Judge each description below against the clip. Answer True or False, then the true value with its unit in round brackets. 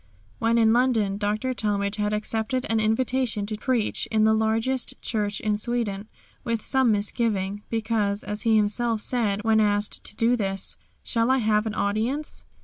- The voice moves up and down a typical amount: False (2.0 semitones)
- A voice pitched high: True (220 Hz)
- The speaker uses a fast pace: False (165 wpm)